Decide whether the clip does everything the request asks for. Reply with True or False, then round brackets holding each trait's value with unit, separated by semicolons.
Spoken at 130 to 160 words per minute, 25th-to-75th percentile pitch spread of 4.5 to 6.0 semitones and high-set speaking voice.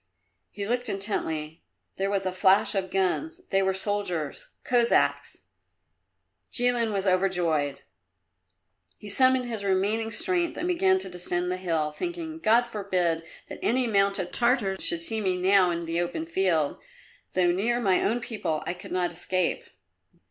True (150 wpm; 4.8 semitones; 195 Hz)